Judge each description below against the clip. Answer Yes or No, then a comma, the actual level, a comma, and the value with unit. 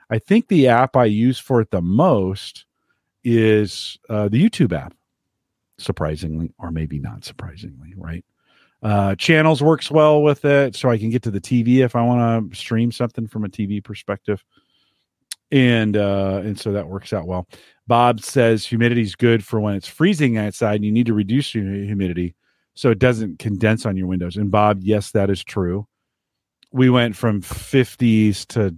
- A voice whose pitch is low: Yes, low, 110 Hz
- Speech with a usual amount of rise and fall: Yes, average, 3.5 semitones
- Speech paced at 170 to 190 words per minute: Yes, average, 180 wpm